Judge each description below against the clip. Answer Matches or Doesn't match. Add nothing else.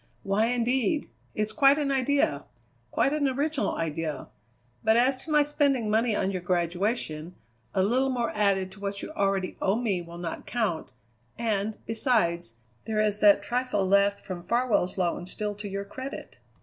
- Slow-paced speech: Doesn't match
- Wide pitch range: Doesn't match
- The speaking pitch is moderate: Doesn't match